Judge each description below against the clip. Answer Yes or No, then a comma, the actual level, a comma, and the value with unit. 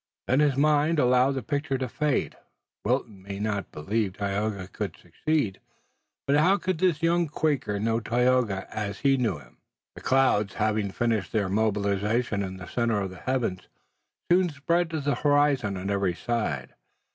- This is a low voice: Yes, low, 115 Hz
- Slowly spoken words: No, average, 165 wpm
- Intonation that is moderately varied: No, wide, 6.1 semitones